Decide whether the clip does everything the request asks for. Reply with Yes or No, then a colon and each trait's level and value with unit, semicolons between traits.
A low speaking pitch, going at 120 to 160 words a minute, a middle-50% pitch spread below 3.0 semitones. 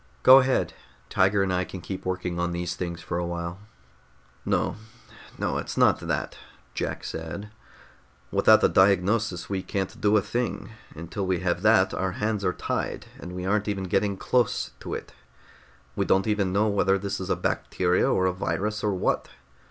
No: very low, 95 Hz; average, 180 wpm; narrow, 2.4 semitones